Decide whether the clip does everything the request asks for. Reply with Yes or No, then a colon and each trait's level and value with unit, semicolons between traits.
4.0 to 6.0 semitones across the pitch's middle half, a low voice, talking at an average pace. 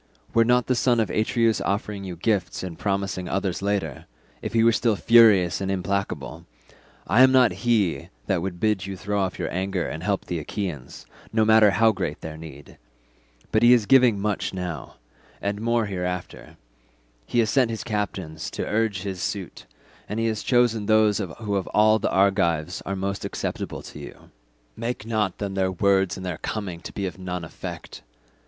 No: average, 3.2 semitones; low, 100 Hz; average, 180 wpm